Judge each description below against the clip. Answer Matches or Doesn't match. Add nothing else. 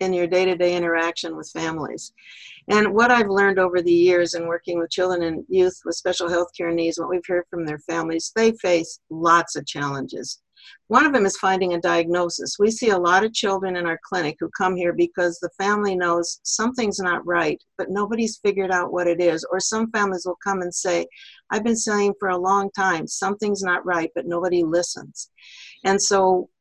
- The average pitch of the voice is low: Doesn't match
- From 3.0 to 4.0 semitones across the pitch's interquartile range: Doesn't match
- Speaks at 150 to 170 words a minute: Doesn't match